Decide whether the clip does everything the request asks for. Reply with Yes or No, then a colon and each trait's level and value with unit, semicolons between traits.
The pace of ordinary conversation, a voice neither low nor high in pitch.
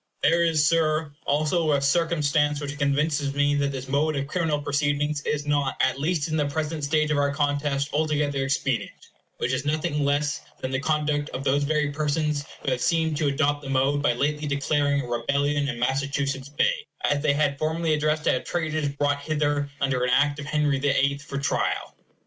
Yes: average, 195 wpm; medium, 145 Hz